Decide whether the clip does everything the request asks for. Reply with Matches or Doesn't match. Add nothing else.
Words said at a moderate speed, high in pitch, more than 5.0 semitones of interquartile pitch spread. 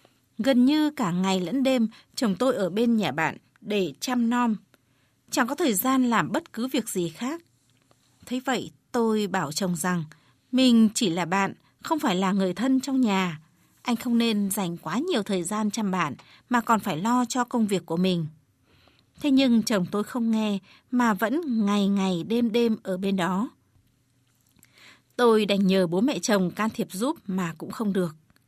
Matches